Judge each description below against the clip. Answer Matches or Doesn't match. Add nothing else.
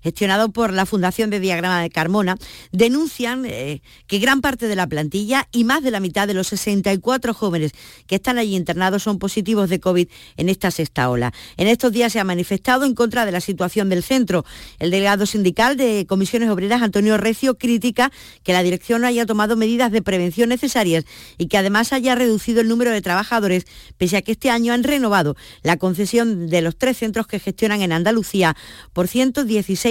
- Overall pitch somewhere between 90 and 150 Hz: Doesn't match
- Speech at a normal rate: Doesn't match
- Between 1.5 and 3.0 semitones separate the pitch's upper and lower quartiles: Doesn't match